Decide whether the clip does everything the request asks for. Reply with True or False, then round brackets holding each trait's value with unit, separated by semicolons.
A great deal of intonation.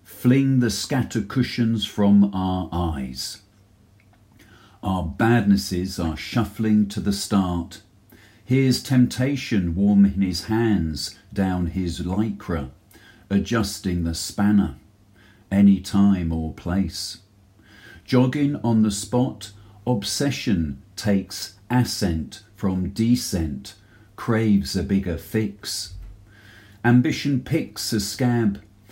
False (2.7 semitones)